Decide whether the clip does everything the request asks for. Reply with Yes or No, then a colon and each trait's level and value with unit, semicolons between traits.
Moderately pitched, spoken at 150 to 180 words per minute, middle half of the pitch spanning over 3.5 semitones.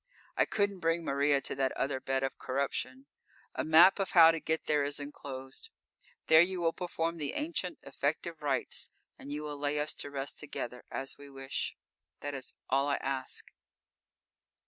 No: medium, 145 Hz; average, 175 wpm; average, 3.2 semitones